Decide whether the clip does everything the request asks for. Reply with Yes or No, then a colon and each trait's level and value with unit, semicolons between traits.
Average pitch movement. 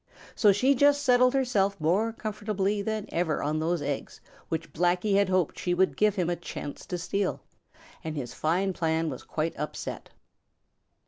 Yes: average, 4.6 semitones